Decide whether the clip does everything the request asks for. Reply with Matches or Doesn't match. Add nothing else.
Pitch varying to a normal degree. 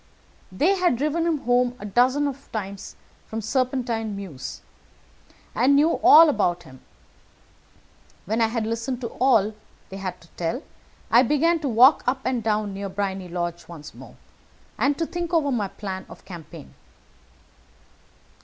Doesn't match